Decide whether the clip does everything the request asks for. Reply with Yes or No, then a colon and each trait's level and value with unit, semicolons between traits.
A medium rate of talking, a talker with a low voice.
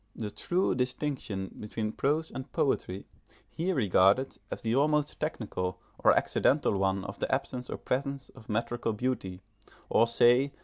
Yes: average, 145 wpm; low, 125 Hz